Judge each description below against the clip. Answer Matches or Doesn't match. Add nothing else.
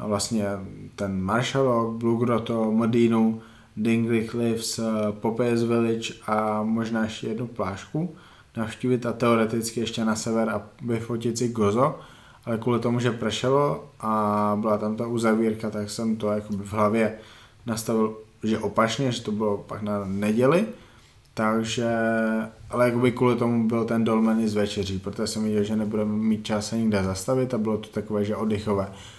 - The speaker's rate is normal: Matches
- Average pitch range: Doesn't match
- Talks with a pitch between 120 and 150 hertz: Doesn't match